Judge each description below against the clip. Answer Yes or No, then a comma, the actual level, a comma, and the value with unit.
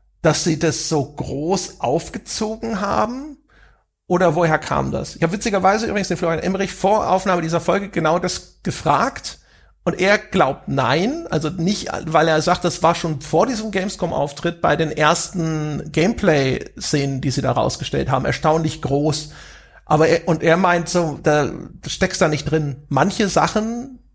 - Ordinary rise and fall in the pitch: Yes, average, 3.7 semitones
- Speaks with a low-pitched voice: No, medium, 170 Hz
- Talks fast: No, average, 160 wpm